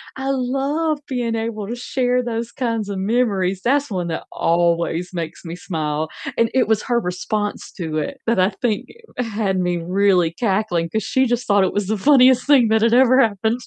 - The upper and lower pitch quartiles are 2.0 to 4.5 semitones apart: No, average, 5.2 semitones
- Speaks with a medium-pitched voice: No, high, 220 Hz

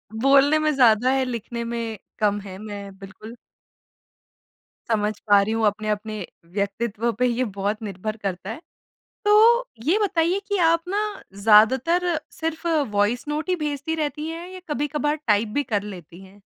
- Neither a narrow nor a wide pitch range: No, wide, 6.7 semitones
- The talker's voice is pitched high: Yes, high, 235 Hz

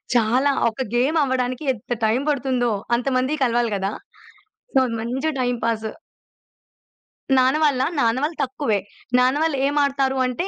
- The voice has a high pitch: Yes, very high, 255 Hz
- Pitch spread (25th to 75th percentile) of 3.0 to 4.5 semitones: No, narrow, 2.5 semitones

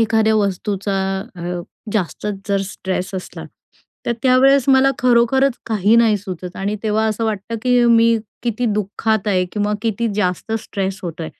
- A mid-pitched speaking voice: No, high, 215 Hz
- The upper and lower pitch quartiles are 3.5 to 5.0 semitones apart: No, average, 3.1 semitones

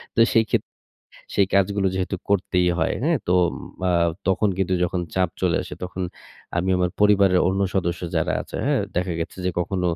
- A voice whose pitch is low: Yes, very low, 95 Hz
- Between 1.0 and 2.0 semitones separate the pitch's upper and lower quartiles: Yes, narrow, 1.6 semitones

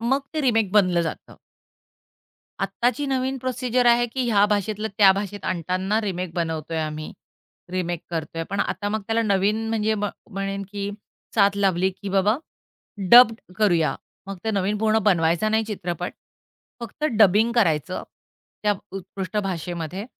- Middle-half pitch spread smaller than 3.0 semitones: No, average, 3.3 semitones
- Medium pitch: No, high, 200 Hz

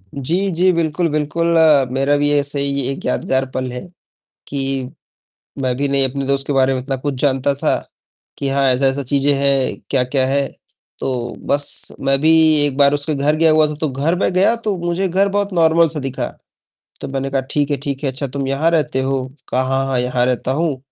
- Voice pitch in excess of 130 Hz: Yes, medium, 140 Hz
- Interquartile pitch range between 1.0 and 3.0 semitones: Yes, narrow, 2.4 semitones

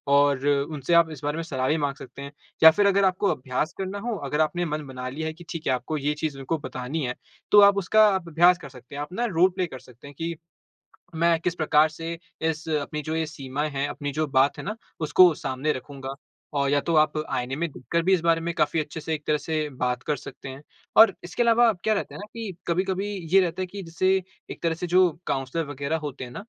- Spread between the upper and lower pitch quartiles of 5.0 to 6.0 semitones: No, average, 3.7 semitones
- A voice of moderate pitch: Yes, medium, 155 Hz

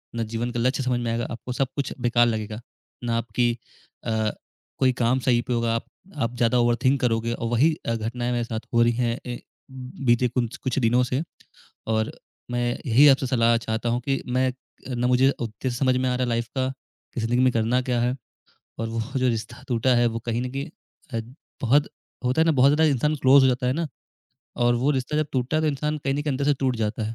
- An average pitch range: No, narrow, 2.0 semitones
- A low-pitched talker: Yes, low, 120 Hz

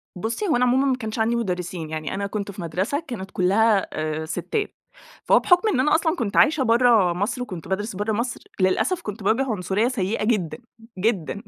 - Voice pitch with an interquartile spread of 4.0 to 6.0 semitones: Yes, average, 4.8 semitones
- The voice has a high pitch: Yes, high, 215 Hz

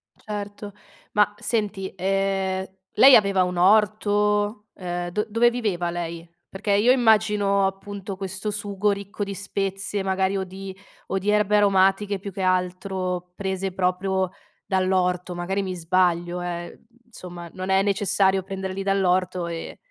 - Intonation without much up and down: Yes, narrow, 1.8 semitones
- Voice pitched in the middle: No, high, 195 Hz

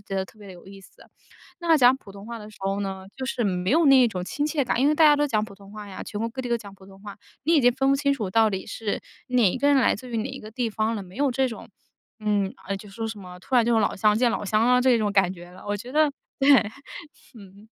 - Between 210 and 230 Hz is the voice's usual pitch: Yes, high, 220 Hz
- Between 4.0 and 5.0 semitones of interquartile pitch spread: Yes, average, 4.6 semitones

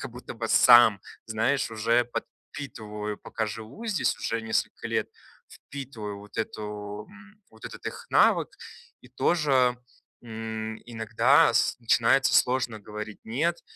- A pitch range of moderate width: Yes, average, 3.1 semitones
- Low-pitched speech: Yes, low, 115 Hz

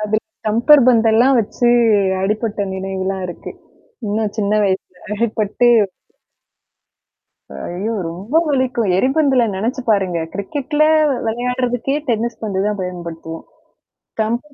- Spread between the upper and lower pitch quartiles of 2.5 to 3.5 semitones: No, average, 4.2 semitones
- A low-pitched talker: No, high, 220 Hz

